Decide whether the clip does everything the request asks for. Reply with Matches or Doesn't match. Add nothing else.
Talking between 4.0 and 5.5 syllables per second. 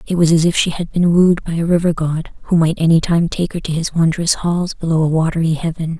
Doesn't match